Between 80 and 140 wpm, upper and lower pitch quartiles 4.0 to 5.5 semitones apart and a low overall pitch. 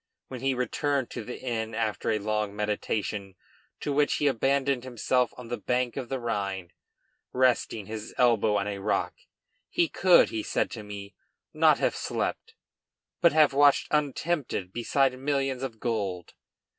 No: average, 155 wpm; average, 4.3 semitones; low, 120 Hz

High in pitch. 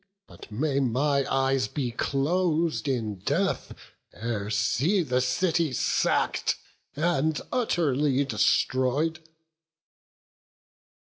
No: low, 135 Hz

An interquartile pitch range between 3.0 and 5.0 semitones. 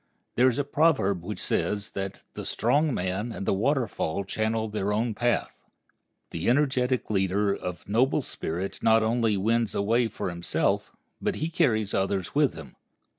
Yes: average, 3.9 semitones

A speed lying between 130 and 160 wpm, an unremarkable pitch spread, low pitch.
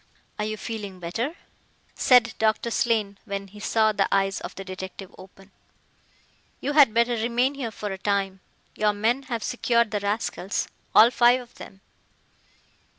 No: average, 155 wpm; average, 3.0 semitones; high, 215 Hz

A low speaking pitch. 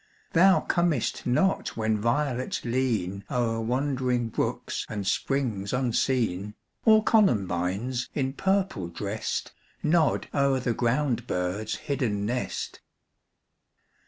Yes: low, 125 Hz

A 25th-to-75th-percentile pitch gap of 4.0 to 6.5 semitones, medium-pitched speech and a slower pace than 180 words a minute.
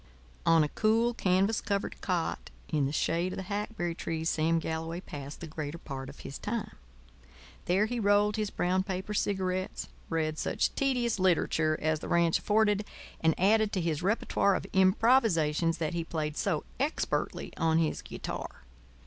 Yes: average, 4.4 semitones; medium, 180 Hz; average, 165 wpm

